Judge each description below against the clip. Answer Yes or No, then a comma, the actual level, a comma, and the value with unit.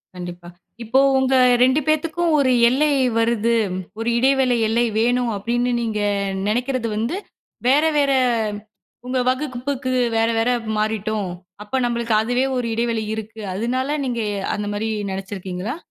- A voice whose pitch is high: Yes, high, 235 Hz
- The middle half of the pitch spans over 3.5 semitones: No, average, 3.0 semitones